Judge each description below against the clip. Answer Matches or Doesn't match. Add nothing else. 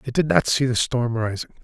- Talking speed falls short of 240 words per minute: Doesn't match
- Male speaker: Matches